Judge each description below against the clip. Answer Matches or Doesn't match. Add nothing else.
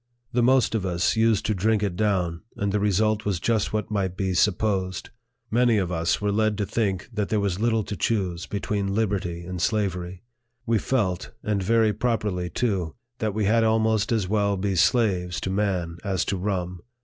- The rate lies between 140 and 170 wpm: Doesn't match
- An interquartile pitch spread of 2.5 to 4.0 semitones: Matches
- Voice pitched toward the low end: Matches